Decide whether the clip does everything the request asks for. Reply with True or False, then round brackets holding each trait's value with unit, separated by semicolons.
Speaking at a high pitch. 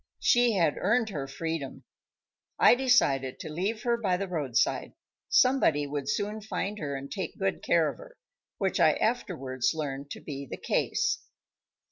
False (170 Hz)